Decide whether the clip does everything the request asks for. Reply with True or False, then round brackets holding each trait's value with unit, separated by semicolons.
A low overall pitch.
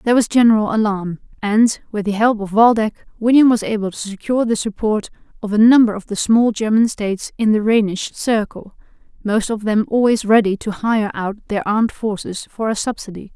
False (215 Hz)